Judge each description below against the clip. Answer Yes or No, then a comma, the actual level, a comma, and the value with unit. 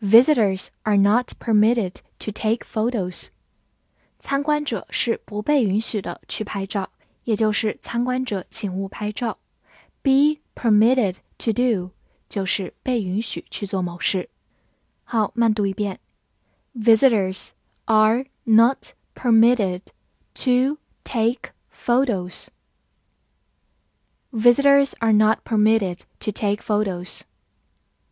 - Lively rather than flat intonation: No, average, 4.0 semitones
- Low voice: No, high, 215 Hz